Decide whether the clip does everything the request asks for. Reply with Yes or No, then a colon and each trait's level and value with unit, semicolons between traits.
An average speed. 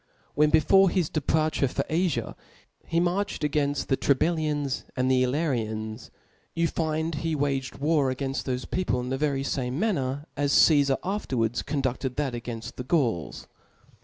Yes: average, 165 wpm